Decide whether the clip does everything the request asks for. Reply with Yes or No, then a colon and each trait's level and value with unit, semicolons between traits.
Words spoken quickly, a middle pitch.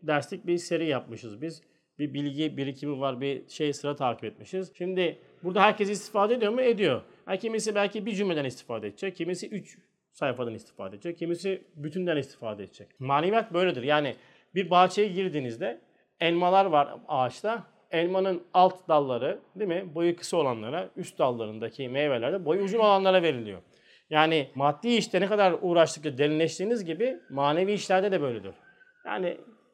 Yes: fast, 145 wpm; medium, 170 Hz